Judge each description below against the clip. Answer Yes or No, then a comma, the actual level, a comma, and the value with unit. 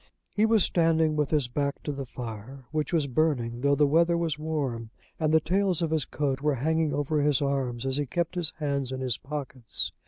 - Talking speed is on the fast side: Yes, fast, 215 wpm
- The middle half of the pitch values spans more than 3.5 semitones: No, average, 3.2 semitones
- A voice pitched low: No, medium, 145 Hz